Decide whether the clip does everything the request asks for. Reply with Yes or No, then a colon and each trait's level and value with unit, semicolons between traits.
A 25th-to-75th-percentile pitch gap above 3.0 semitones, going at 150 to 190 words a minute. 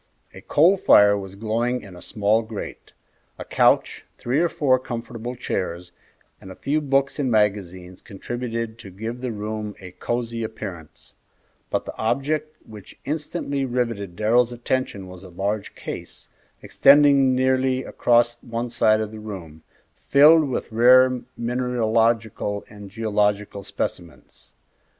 No: average, 3.8 semitones; slow, 135 wpm